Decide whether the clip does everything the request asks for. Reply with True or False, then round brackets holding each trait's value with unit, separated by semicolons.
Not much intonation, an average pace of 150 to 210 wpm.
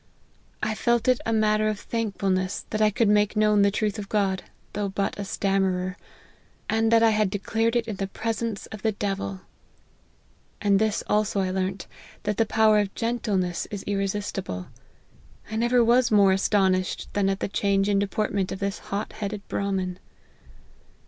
True (2.0 semitones; 175 wpm)